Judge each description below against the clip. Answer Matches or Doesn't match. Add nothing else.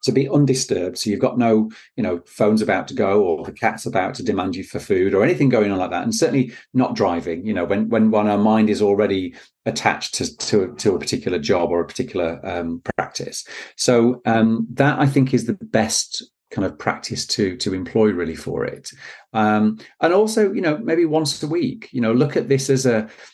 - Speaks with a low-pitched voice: Matches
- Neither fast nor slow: Doesn't match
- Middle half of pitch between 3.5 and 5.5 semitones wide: Matches